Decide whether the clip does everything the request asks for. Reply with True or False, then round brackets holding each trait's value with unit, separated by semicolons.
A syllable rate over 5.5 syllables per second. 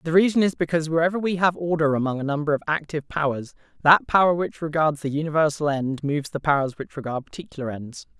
True (6.6 syllables/s)